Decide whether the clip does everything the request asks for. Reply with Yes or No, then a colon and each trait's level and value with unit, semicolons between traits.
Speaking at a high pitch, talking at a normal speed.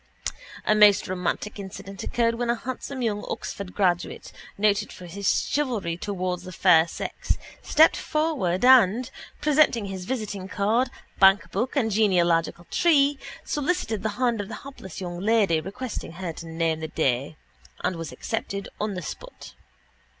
Yes: high, 200 Hz; average, 150 wpm